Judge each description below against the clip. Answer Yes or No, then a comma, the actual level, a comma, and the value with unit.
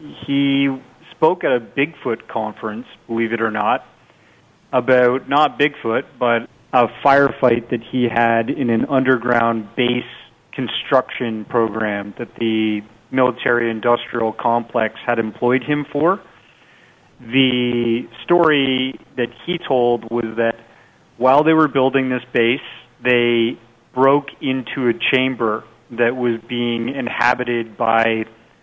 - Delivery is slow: Yes, slow, 120 wpm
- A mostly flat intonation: Yes, narrow, 2.2 semitones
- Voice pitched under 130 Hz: Yes, low, 120 Hz